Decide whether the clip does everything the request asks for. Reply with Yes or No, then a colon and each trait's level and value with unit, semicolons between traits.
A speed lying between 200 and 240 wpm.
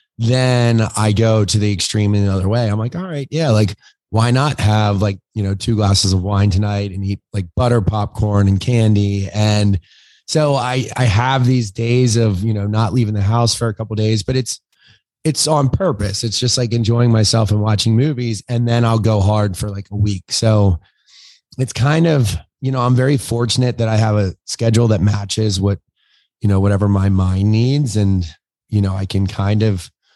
Yes: fast, 205 wpm